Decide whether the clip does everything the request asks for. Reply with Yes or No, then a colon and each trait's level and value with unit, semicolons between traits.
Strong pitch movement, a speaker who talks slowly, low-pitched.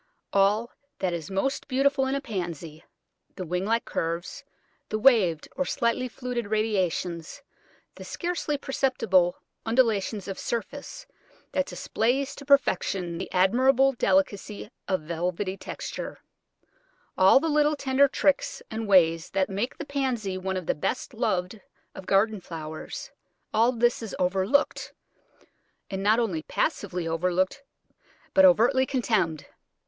No: wide, 6.2 semitones; slow, 130 wpm; high, 215 Hz